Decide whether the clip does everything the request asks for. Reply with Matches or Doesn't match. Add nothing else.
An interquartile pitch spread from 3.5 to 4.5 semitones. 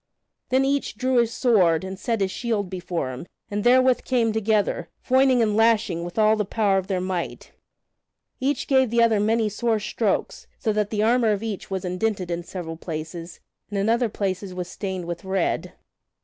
Matches